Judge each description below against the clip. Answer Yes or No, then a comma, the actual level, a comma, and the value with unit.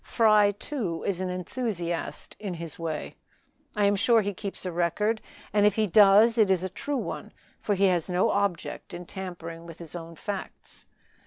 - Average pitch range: Yes, average, 3.3 semitones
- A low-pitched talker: No, high, 190 Hz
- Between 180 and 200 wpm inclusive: Yes, average, 185 wpm